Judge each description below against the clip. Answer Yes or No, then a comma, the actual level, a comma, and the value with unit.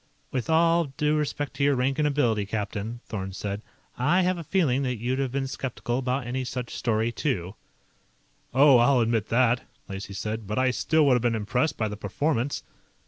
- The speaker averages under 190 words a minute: No, average, 195 wpm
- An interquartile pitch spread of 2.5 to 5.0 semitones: Yes, average, 4.1 semitones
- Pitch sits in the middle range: No, low, 125 Hz